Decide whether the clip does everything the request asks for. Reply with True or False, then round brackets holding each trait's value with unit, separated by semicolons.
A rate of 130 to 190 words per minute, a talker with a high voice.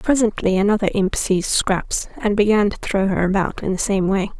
False (205 wpm; 200 Hz)